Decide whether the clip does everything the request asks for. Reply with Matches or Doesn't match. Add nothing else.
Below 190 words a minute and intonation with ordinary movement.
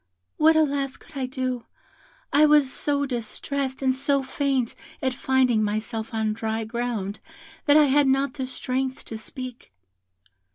Matches